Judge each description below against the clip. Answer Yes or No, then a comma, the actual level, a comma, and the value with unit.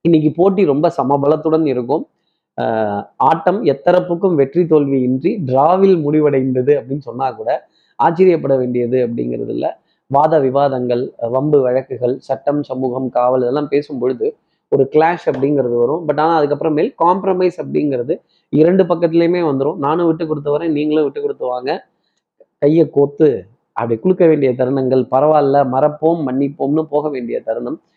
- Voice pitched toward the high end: No, medium, 145 Hz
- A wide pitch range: No, average, 3.8 semitones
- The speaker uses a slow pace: No, fast, 130 wpm